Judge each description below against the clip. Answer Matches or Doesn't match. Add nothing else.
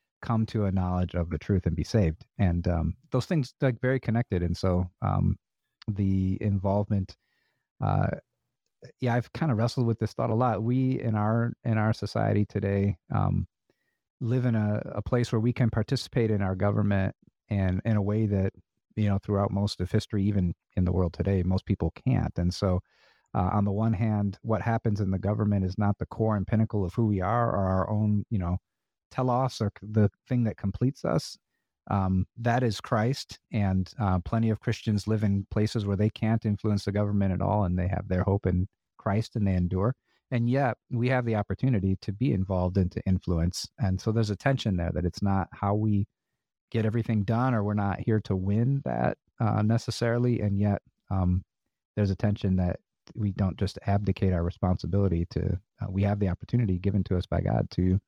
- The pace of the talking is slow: Doesn't match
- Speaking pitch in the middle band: Doesn't match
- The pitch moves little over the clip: Doesn't match